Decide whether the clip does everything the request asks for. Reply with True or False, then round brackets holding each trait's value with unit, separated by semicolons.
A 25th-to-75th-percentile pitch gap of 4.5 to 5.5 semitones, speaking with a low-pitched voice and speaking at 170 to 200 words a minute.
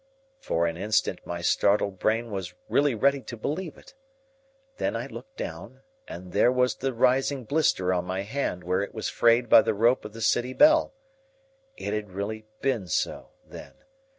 True (5.1 semitones; 110 Hz; 180 wpm)